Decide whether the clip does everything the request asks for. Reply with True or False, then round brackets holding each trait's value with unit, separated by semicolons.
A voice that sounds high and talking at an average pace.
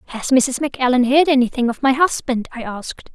True (260 Hz; 190 wpm)